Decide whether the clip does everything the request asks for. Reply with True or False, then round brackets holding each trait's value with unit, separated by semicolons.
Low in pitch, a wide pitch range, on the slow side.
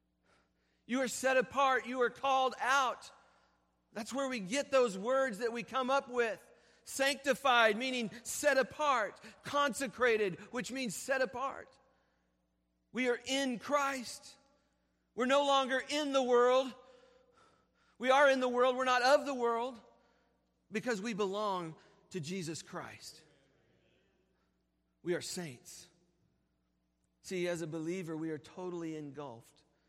False (240 Hz; 7.8 semitones; 130 wpm)